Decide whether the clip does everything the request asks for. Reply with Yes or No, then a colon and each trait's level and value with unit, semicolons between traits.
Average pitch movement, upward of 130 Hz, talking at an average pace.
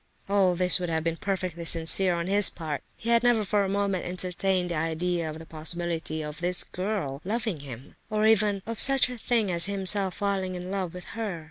No: average, 3.2 semitones; medium, 185 Hz; fast, 210 wpm